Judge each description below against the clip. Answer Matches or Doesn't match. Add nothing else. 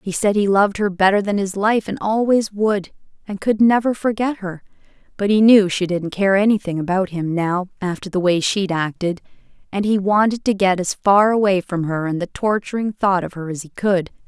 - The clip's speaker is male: Doesn't match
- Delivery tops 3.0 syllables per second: Matches